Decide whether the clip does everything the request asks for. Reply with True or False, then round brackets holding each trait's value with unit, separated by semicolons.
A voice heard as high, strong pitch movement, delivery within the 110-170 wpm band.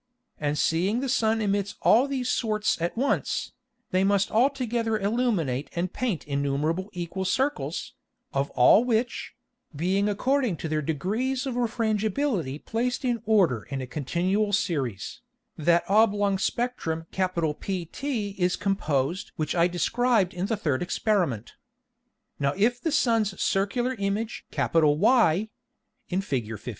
True (200 Hz; 5.9 semitones; 135 wpm)